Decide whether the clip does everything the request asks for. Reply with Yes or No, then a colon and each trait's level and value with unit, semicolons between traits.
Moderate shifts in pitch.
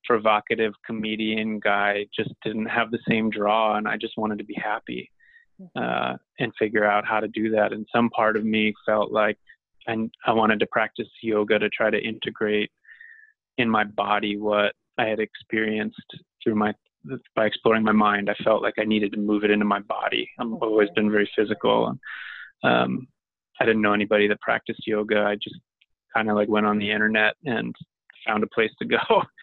No: narrow, 0.9 semitones